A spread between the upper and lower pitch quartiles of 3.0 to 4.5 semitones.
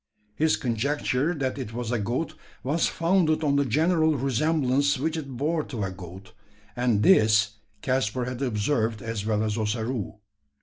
No: average, 5.2 semitones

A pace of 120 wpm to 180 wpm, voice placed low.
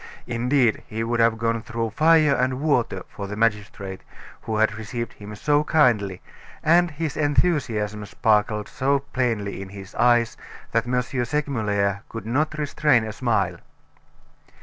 Yes: average, 145 wpm; low, 115 Hz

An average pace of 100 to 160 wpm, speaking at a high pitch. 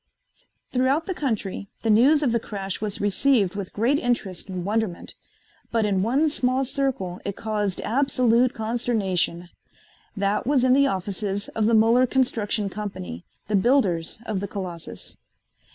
Yes: average, 150 wpm; high, 215 Hz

